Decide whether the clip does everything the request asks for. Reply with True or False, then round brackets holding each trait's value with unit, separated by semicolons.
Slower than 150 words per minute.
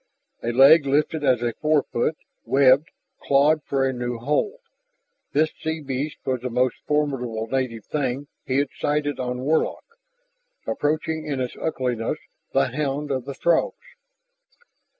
True (140 wpm)